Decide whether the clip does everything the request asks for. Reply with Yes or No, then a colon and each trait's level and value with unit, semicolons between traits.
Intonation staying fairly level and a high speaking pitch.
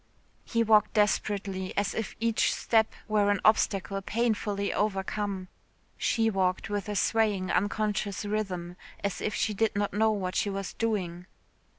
Yes: narrow, 1.8 semitones; high, 205 Hz